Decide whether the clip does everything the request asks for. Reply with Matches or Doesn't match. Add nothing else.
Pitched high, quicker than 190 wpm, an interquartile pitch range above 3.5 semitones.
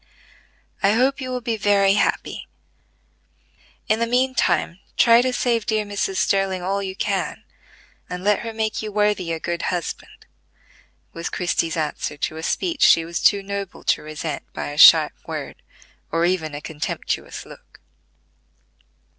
Doesn't match